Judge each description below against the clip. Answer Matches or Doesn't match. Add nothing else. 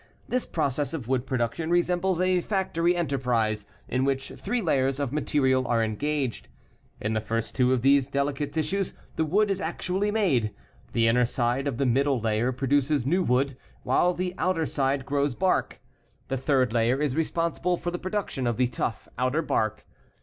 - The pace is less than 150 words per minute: Doesn't match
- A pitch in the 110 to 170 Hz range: Matches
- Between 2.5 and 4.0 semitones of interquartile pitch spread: Doesn't match